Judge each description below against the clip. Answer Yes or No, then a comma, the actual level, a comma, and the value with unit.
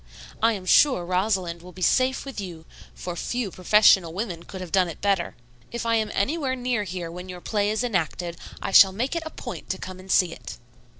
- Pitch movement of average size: Yes, average, 4.3 semitones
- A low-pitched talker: No, high, 190 Hz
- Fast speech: Yes, fast, 215 wpm